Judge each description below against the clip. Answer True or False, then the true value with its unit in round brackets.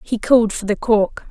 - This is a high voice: True (220 Hz)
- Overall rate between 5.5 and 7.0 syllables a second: False (5.1 syllables/s)